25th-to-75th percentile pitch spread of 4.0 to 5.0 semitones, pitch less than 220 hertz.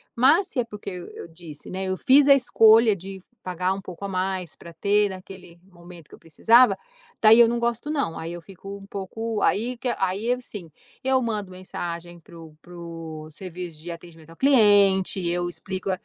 Yes: average, 4.5 semitones; high, 190 Hz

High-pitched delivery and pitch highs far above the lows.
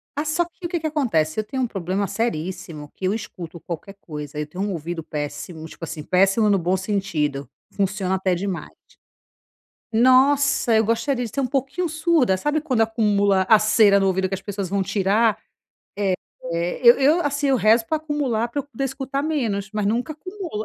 Yes: high, 215 Hz; wide, 6.5 semitones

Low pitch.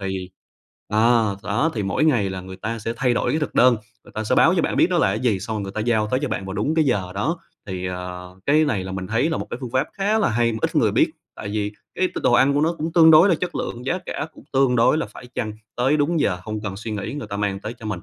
Yes: low, 115 Hz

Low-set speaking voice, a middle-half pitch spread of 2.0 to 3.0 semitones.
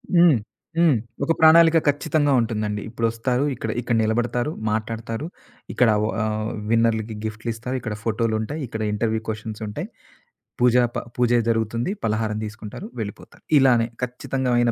Yes: low, 115 Hz; narrow, 2.4 semitones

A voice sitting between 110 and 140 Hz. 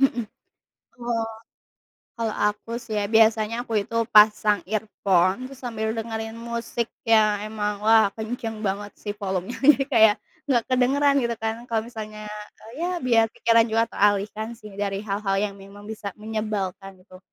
No: high, 220 Hz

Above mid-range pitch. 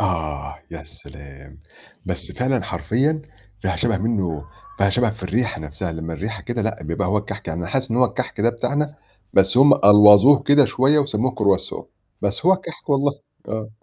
No: low, 105 Hz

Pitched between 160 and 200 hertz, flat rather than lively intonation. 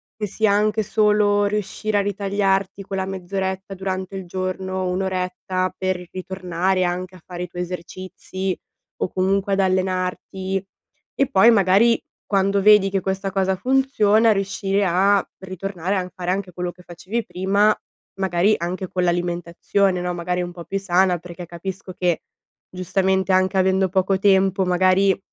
Yes: high, 190 Hz; narrow, 1.4 semitones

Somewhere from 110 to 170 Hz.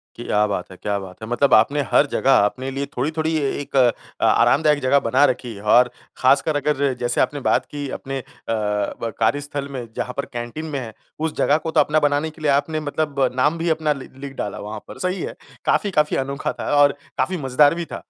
Yes: medium, 140 Hz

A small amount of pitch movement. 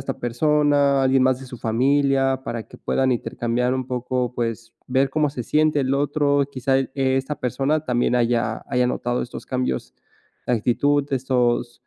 Yes: narrow, 2.3 semitones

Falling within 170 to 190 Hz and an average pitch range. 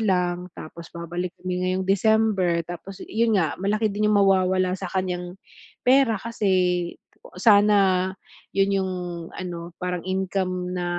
No: medium, 185 Hz; narrow, 2.0 semitones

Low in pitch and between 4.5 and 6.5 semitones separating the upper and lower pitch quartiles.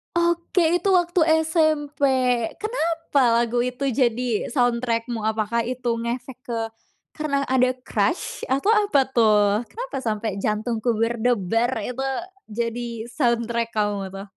No: high, 245 Hz; average, 4.8 semitones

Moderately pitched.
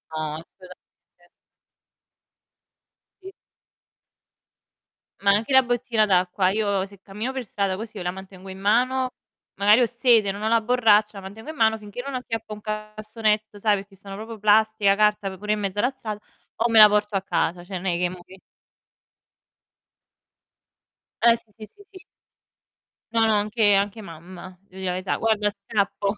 No: high, 210 Hz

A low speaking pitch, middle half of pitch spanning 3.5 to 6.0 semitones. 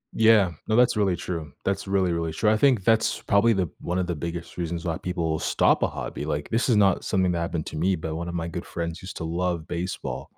No: very low, 90 Hz; average, 2.9 semitones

